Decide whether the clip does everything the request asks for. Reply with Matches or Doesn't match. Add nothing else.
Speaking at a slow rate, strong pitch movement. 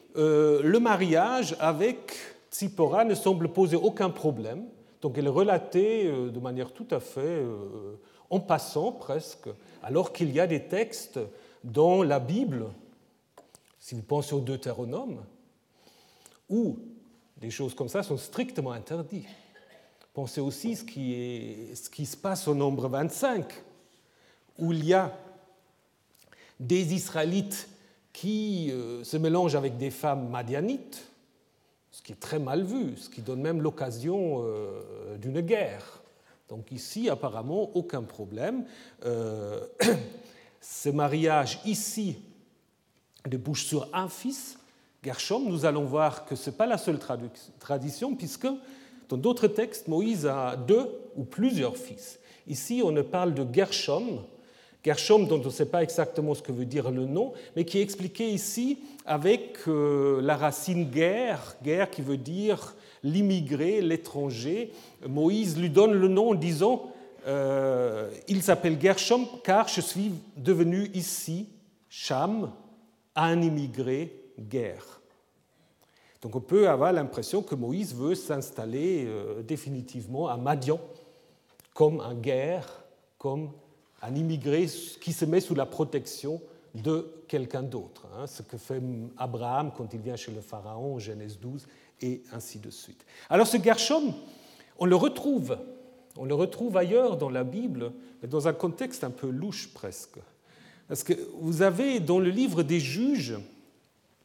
Matches